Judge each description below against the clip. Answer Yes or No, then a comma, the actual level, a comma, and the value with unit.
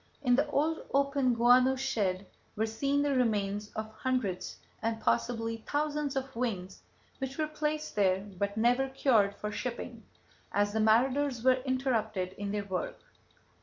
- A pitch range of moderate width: Yes, average, 4.2 semitones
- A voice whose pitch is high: Yes, high, 240 Hz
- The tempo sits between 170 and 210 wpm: No, average, 150 wpm